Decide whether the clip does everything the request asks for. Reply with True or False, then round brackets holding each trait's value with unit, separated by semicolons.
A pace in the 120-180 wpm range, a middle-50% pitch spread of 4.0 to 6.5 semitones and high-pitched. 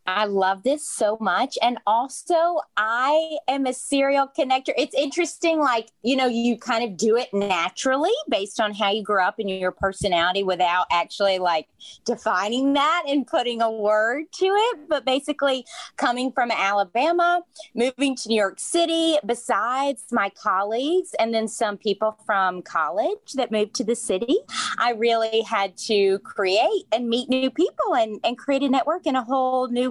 True (170 wpm; 5.1 semitones; 245 Hz)